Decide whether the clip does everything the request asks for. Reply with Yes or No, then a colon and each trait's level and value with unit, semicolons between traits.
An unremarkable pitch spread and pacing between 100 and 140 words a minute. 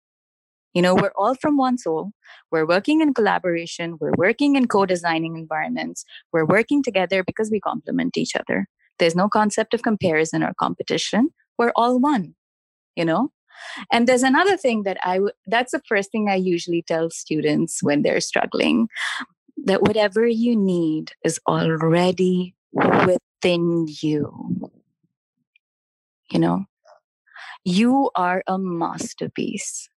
No: wide, 6.2 semitones; slow, 135 wpm